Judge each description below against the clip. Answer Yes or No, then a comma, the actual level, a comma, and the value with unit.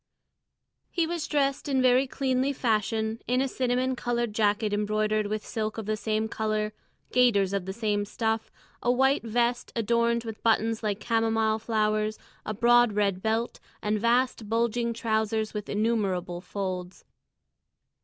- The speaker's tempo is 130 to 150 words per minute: Yes, average, 145 wpm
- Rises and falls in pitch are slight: Yes, narrow, 2.2 semitones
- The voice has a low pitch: No, high, 220 Hz